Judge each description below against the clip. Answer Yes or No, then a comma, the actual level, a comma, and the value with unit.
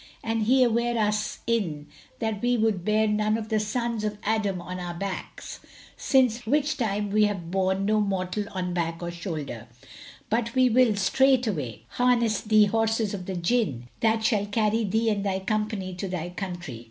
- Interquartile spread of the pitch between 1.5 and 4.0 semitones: Yes, average, 3.4 semitones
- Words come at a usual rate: Yes, average, 175 wpm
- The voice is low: No, high, 210 Hz